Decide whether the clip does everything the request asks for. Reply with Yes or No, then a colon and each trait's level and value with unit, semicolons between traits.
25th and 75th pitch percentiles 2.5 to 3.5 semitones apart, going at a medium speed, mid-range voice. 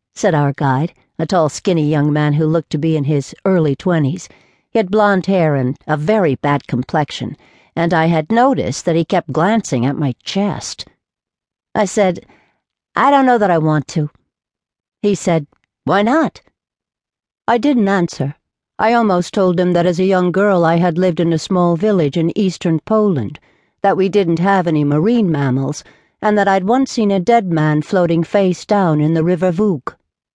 No: average, 4.8 semitones; average, 185 wpm; medium, 175 Hz